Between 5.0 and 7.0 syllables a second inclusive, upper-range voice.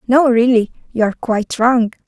Yes: 5.8 syllables/s; high, 235 Hz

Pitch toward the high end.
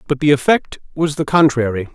No: medium, 140 Hz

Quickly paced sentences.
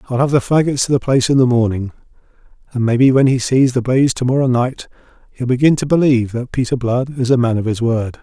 Yes: fast, 240 wpm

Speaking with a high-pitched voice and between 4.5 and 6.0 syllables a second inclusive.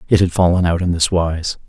No: very low, 85 Hz; 5.6 syllables/s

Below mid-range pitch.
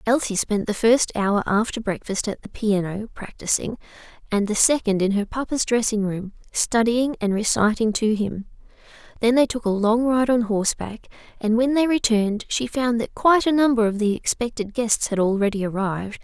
No: high, 225 Hz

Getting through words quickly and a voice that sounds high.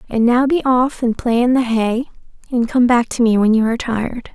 Yes: fast, 250 wpm; high, 240 Hz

